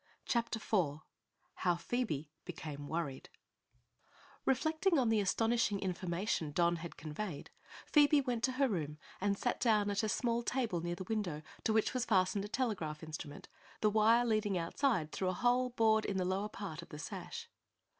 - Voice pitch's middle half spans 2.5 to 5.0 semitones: No, wide, 5.5 semitones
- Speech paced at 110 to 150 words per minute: No, average, 170 wpm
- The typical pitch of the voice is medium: No, high, 205 Hz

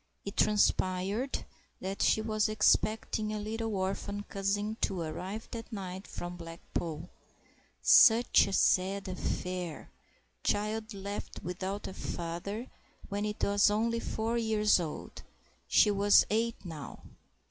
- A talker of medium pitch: No, high, 200 Hz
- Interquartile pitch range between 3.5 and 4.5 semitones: No, average, 2.8 semitones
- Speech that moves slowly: Yes, slow, 115 wpm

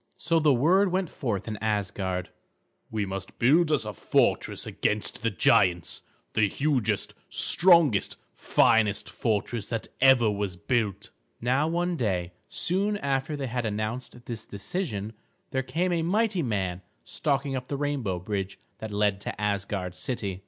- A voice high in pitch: No, low, 115 Hz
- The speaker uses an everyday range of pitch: No, wide, 6.3 semitones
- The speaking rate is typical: Yes, average, 145 wpm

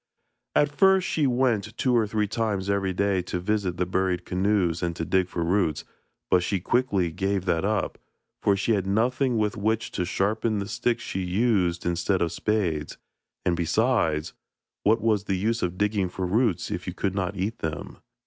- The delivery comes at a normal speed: Yes, average, 185 wpm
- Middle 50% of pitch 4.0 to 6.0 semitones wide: No, average, 3.6 semitones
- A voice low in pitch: Yes, low, 100 Hz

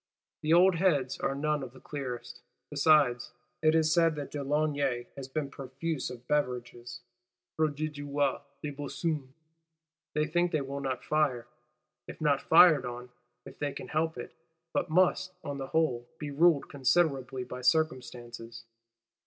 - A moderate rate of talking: Yes, average, 145 wpm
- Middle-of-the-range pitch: Yes, medium, 145 Hz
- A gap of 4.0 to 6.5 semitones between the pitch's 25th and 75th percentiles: No, average, 3.4 semitones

